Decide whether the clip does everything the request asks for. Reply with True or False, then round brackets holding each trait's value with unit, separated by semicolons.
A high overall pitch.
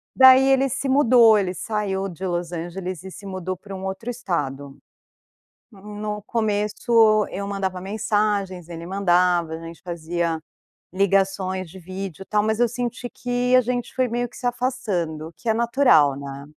True (195 Hz)